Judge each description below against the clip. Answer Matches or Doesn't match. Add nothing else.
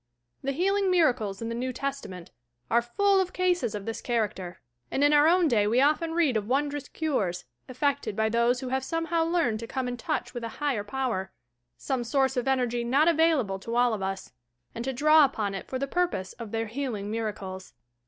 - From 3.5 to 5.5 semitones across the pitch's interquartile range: Matches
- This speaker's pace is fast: Matches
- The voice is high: Matches